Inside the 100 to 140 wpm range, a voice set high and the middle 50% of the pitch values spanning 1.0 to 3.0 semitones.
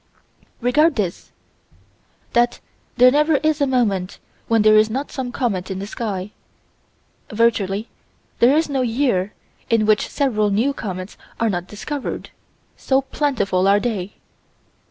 No: slow, 135 wpm; high, 230 Hz; average, 4.8 semitones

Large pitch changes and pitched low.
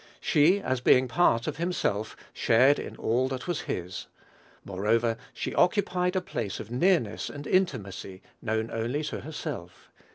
Yes: wide, 7.2 semitones; low, 125 Hz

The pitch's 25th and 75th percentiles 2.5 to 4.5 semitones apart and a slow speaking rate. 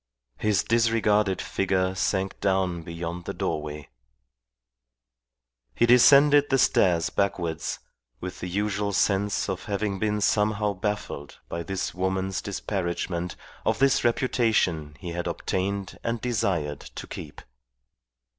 Yes: average, 3.3 semitones; slow, 120 wpm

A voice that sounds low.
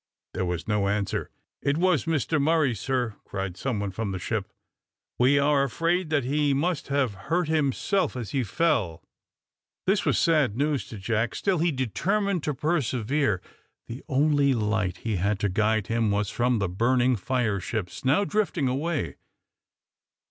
Yes: low, 130 Hz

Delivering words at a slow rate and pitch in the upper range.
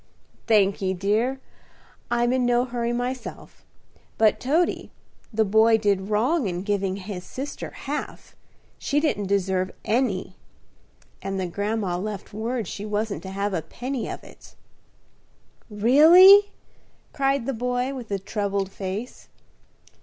Yes: slow, 130 wpm; high, 220 Hz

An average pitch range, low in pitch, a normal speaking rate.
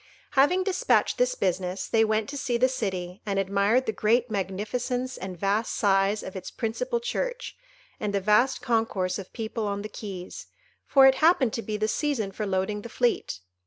No: average, 4.2 semitones; high, 215 Hz; average, 185 wpm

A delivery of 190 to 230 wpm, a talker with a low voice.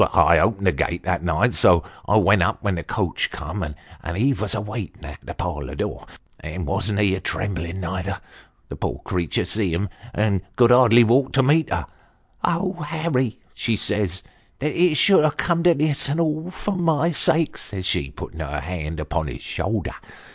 Yes: average, 200 wpm; low, 105 Hz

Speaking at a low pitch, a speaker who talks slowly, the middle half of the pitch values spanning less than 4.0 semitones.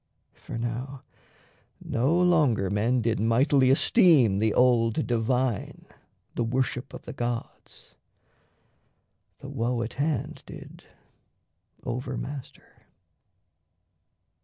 Yes: low, 125 Hz; slow, 95 wpm; average, 2.8 semitones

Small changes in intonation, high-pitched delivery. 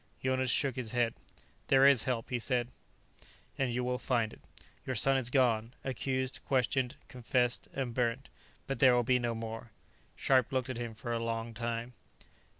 No: narrow, 1.9 semitones; low, 125 Hz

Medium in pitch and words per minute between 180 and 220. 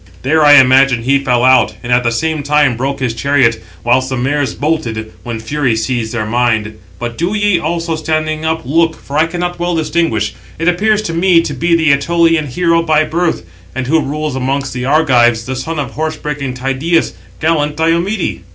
Yes: medium, 145 Hz; average, 195 wpm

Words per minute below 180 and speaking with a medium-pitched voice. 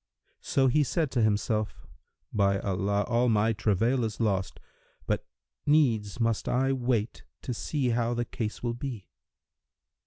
No: average, 145 wpm; low, 115 Hz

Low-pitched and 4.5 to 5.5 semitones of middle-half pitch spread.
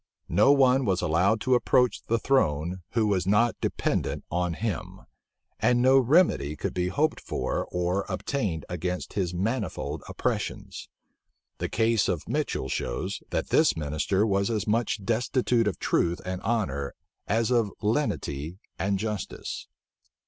Yes: low, 100 Hz; average, 4.8 semitones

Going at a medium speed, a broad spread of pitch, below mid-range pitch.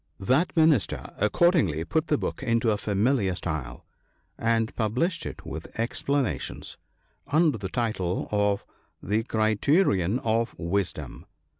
No: slow, 120 wpm; wide, 5.7 semitones; low, 110 Hz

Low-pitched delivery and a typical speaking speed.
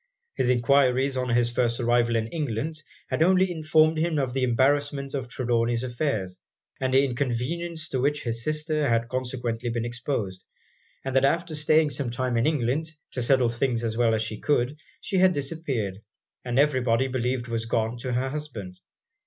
Yes: low, 130 Hz; average, 175 wpm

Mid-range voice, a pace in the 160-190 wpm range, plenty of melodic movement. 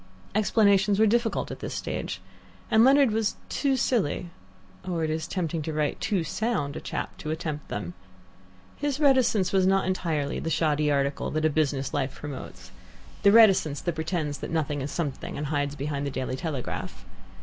Yes: medium, 160 Hz; average, 175 wpm; wide, 5.9 semitones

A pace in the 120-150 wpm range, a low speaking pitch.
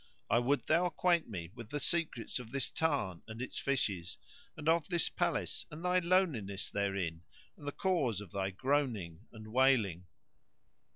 No: average, 165 wpm; low, 125 Hz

